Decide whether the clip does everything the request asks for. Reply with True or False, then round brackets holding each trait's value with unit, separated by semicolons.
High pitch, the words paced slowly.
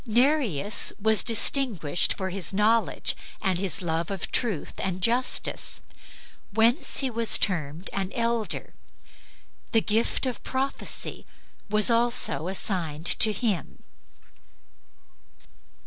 True (215 Hz; 105 wpm)